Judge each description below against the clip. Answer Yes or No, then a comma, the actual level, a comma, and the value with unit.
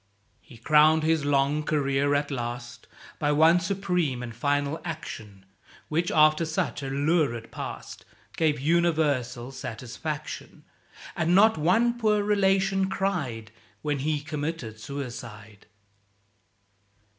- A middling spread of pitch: Yes, average, 4.3 semitones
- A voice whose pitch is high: No, medium, 150 Hz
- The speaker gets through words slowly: Yes, slow, 115 wpm